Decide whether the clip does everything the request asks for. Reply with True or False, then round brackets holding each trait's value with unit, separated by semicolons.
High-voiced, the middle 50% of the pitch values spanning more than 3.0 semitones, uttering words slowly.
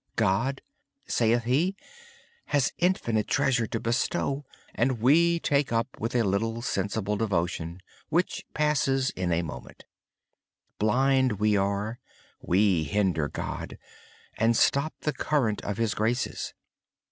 False (115 Hz; 4.8 semitones; 125 wpm)